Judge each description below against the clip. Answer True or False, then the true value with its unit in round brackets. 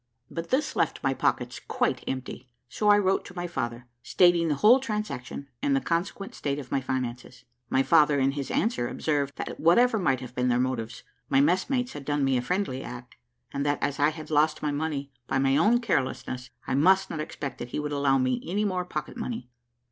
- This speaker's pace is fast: True (210 wpm)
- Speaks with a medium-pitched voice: True (145 Hz)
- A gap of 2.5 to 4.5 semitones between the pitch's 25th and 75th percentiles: False (5.5 semitones)